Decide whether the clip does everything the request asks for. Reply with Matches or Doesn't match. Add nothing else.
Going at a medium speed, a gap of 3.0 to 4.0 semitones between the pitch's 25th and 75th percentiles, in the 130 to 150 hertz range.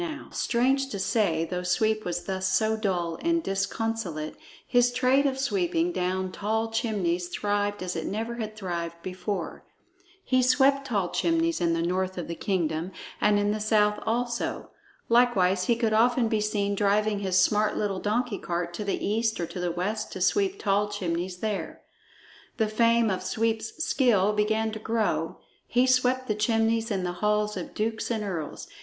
Doesn't match